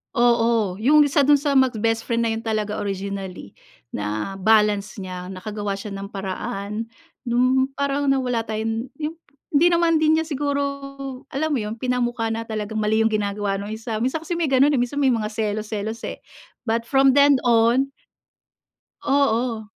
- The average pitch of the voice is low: No, high, 225 Hz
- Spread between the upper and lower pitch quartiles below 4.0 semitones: No, average, 4.3 semitones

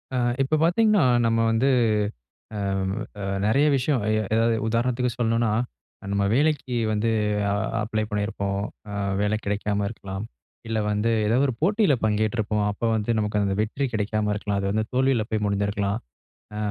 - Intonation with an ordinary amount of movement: Yes, average, 3.3 semitones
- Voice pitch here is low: Yes, low, 110 Hz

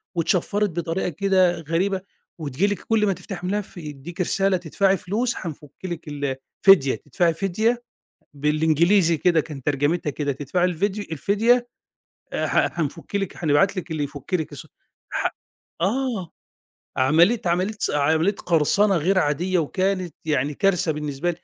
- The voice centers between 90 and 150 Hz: No, medium, 175 Hz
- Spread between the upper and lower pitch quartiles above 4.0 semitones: Yes, average, 4.4 semitones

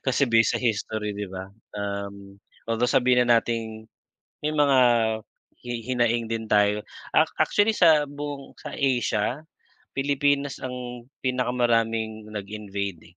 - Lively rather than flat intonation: No, average, 3.9 semitones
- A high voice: No, low, 115 Hz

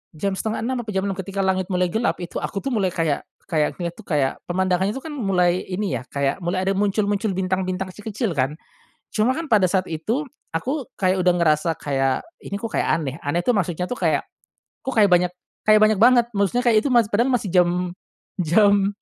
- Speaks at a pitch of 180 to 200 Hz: Yes, high, 190 Hz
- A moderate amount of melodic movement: Yes, average, 3.6 semitones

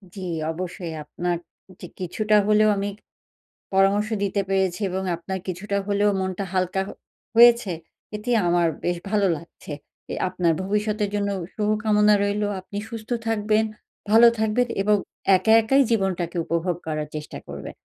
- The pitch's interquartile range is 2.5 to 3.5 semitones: Yes, average, 2.8 semitones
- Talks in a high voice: Yes, high, 200 Hz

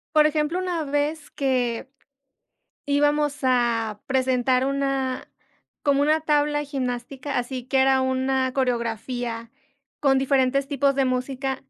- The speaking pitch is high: Yes, very high, 265 Hz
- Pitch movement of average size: No, narrow, 2.2 semitones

